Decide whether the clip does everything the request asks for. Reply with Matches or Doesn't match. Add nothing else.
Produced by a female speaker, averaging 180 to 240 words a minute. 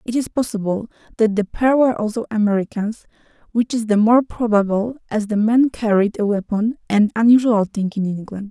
Doesn't match